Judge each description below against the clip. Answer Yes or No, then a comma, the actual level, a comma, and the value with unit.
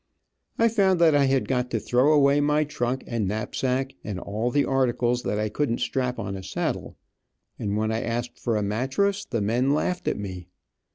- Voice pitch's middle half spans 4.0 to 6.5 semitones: Yes, average, 4.7 semitones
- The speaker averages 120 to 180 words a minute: No, average, 195 wpm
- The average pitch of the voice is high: No, low, 125 Hz